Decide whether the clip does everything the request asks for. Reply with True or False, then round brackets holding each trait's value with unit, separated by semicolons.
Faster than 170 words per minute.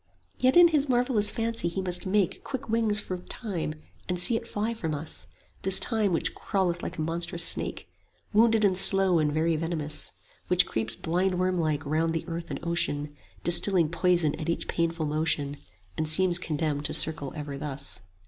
True (180 wpm)